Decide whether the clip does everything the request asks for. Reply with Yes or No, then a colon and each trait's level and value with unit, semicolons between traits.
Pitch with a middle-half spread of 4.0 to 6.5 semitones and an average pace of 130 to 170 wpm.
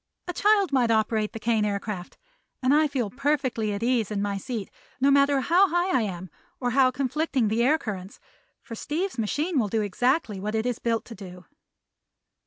No: average, 4.9 semitones; average, 190 wpm